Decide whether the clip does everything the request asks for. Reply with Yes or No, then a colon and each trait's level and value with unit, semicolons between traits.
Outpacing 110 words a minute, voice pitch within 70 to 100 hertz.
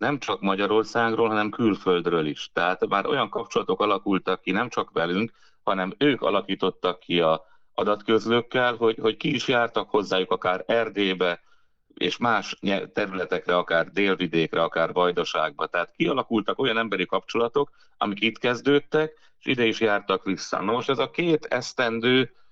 No: average, 150 wpm; low, 110 Hz